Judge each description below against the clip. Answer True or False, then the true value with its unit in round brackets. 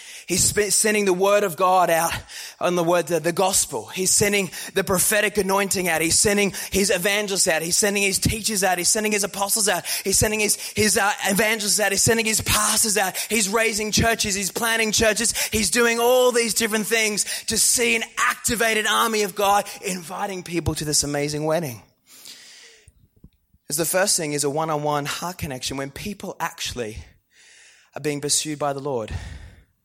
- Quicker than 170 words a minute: True (180 wpm)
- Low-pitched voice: False (200 Hz)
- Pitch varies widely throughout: False (4.3 semitones)